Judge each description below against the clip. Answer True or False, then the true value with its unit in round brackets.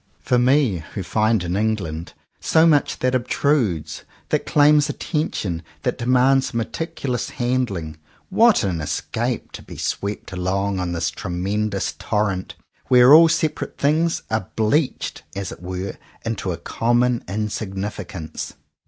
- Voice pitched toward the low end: True (110 Hz)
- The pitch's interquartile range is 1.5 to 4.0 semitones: False (5.6 semitones)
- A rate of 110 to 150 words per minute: True (135 wpm)